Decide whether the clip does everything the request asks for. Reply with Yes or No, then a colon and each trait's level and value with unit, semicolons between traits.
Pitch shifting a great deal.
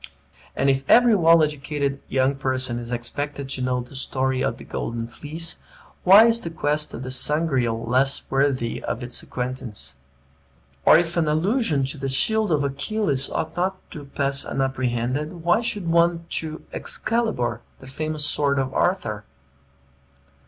No: average, 4.3 semitones